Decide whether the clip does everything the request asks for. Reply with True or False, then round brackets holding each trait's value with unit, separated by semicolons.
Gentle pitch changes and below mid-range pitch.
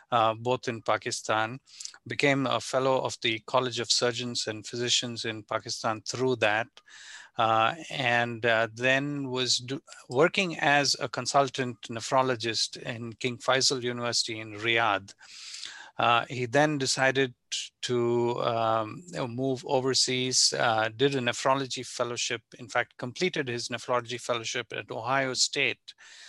True (2.2 semitones; 125 Hz)